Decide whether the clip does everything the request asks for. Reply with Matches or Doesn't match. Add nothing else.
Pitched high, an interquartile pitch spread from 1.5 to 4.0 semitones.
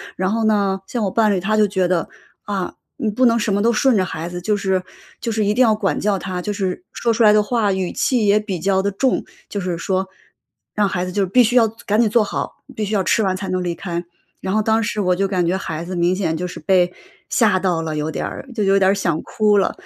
Matches